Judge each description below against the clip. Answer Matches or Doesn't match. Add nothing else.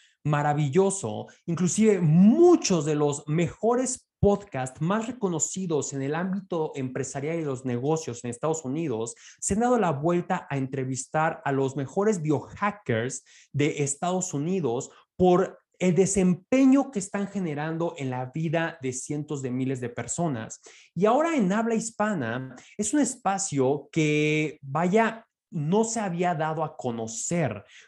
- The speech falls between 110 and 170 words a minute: Matches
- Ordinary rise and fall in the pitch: Doesn't match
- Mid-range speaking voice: Matches